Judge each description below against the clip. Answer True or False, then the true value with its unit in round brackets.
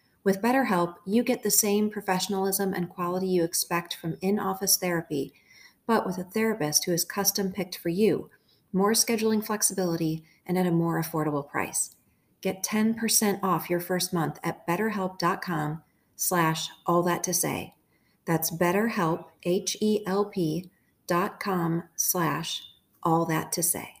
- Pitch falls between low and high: True (180 Hz)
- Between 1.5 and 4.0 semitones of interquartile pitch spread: True (3.1 semitones)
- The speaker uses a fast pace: False (135 wpm)